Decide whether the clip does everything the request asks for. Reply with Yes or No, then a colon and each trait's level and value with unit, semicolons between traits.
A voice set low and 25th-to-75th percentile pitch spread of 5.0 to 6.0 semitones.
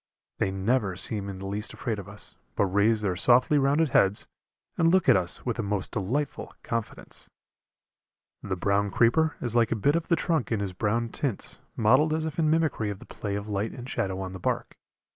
Yes: low, 110 Hz; wide, 5.6 semitones